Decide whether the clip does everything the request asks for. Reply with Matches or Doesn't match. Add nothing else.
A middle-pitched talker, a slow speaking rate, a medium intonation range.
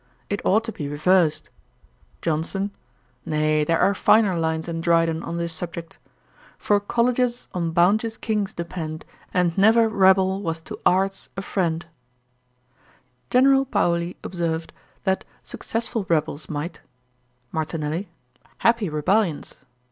Matches